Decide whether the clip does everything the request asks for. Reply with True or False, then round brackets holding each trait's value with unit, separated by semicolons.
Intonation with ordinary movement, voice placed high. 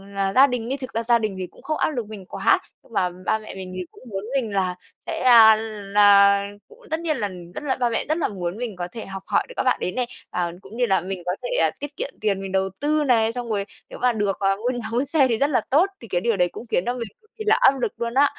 True (4.7 semitones; 220 Hz)